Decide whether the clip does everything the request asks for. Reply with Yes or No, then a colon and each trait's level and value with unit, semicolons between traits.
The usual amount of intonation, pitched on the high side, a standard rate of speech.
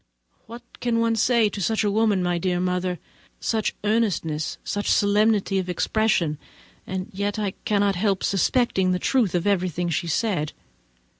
Yes: average, 3.3 semitones; high, 200 Hz; average, 155 wpm